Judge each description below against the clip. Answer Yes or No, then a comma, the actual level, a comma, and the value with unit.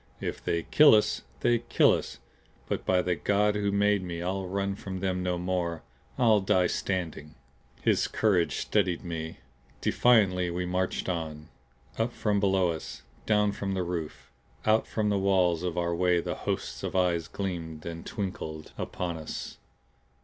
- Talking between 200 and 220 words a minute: No, average, 165 wpm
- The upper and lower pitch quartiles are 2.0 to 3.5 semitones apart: Yes, average, 2.8 semitones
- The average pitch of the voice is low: Yes, very low, 90 Hz